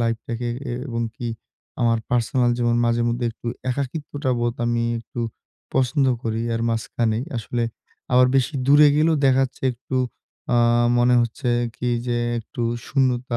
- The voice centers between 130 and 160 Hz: No, low, 120 Hz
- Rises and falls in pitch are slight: Yes, narrow, 1.9 semitones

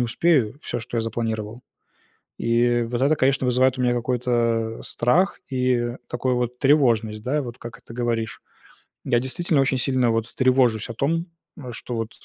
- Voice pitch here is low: Yes, low, 120 Hz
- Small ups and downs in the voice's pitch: Yes, narrow, 2.1 semitones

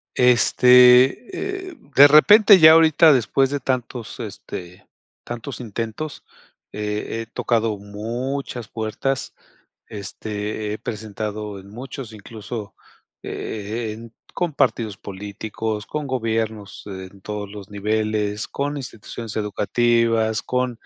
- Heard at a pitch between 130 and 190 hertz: No, low, 115 Hz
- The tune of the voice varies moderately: Yes, average, 3.5 semitones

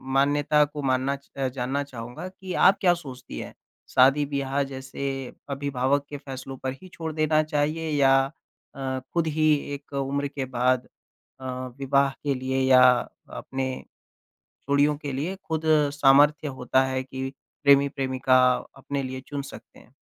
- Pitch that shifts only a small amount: Yes, narrow, 1.9 semitones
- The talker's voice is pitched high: No, medium, 140 Hz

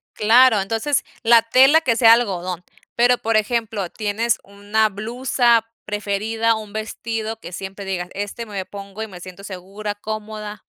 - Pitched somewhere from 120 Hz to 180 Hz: No, high, 215 Hz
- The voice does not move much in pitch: Yes, narrow, 2.2 semitones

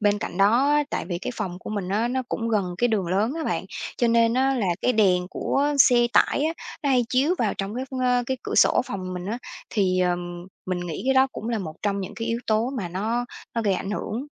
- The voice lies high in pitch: Yes, high, 220 Hz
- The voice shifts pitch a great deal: No, average, 4.9 semitones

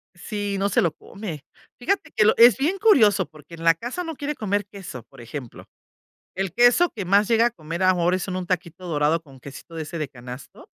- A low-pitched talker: No, medium, 185 Hz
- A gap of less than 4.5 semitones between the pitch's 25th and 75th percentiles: No, wide, 5.5 semitones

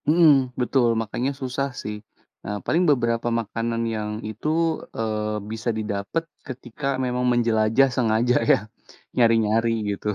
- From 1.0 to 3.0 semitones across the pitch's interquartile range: Yes, narrow, 2.6 semitones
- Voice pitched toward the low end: Yes, low, 115 Hz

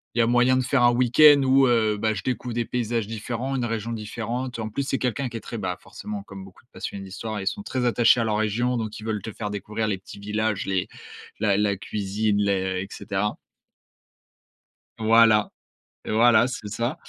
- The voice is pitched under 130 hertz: Yes, low, 110 Hz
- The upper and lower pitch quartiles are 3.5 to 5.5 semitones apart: No, average, 2.7 semitones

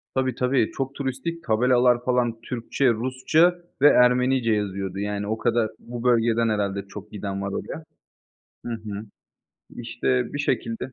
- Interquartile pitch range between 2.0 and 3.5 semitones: Yes, average, 3.1 semitones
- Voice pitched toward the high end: No, low, 120 Hz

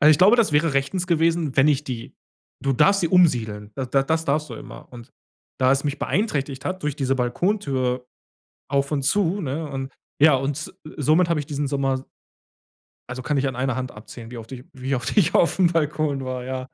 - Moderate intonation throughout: Yes, average, 3.5 semitones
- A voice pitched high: No, medium, 140 Hz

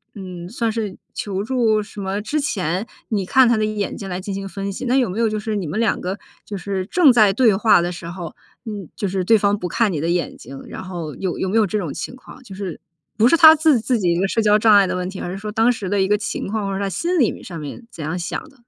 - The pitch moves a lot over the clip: No, average, 3.3 semitones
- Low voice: No, high, 200 Hz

